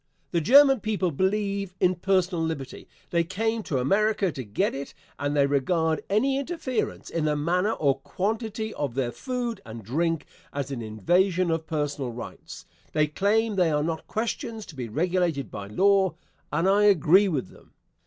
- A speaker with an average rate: Yes, average, 170 wpm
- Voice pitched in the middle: Yes, medium, 175 Hz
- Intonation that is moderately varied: No, wide, 6.0 semitones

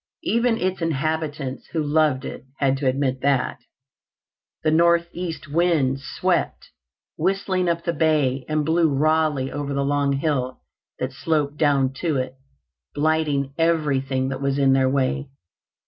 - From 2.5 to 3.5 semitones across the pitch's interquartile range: Yes, average, 3.0 semitones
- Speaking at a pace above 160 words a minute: No, average, 140 wpm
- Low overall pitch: No, medium, 145 Hz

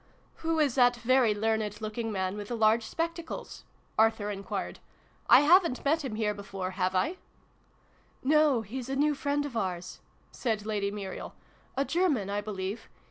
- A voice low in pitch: No, high, 225 Hz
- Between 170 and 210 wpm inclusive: Yes, average, 180 wpm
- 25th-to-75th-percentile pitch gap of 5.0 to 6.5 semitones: Yes, wide, 5.5 semitones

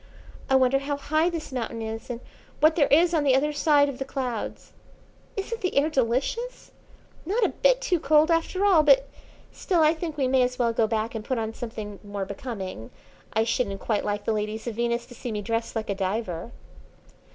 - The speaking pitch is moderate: No, very high, 255 Hz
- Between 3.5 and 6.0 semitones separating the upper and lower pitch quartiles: Yes, wide, 5.6 semitones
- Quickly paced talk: Yes, fast, 210 wpm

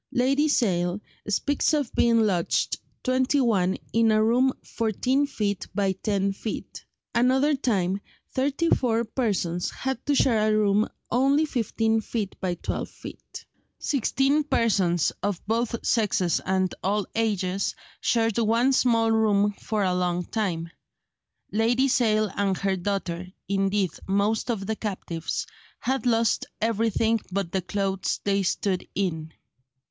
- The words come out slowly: Yes, slow, 130 wpm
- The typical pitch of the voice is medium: No, high, 215 Hz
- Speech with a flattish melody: No, average, 3.7 semitones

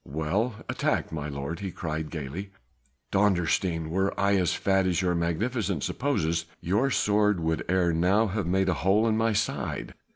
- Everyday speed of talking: Yes, average, 165 wpm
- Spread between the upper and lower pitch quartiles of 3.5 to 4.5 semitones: Yes, average, 3.9 semitones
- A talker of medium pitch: No, very low, 95 Hz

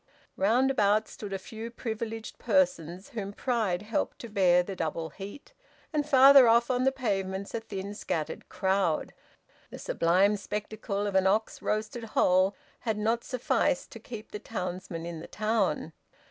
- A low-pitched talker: No, high, 210 Hz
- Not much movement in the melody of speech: No, average, 3.4 semitones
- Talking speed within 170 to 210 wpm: No, average, 160 wpm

